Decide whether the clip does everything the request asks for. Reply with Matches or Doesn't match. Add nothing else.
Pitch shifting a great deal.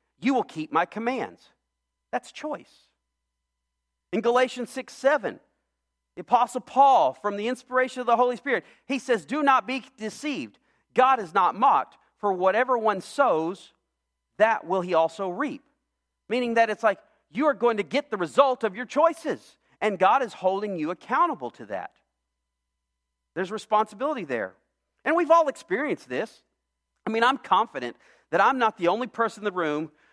Matches